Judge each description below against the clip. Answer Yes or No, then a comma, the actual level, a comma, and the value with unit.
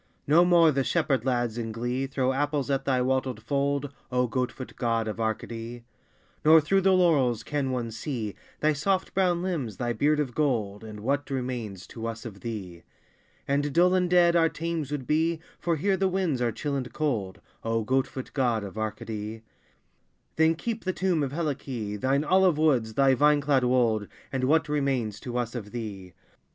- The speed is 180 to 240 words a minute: Yes, average, 190 wpm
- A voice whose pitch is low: Yes, low, 130 Hz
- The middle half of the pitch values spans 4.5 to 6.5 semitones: Yes, average, 4.9 semitones